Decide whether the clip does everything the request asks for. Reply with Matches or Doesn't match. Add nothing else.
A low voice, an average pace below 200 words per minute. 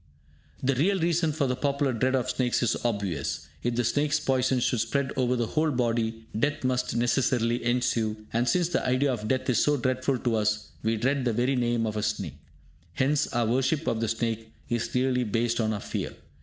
Doesn't match